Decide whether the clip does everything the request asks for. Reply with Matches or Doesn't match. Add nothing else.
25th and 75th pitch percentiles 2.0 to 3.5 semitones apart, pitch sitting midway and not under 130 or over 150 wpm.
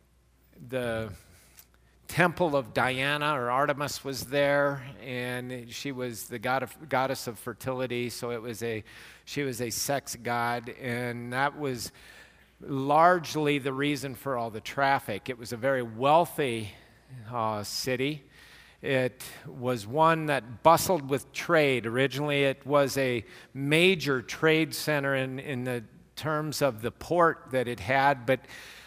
Doesn't match